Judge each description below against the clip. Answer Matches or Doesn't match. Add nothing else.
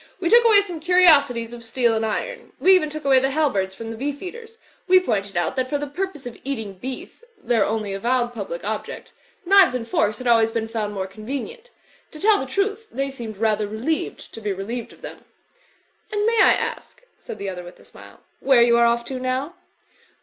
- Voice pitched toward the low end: Doesn't match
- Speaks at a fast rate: Matches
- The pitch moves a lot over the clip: Matches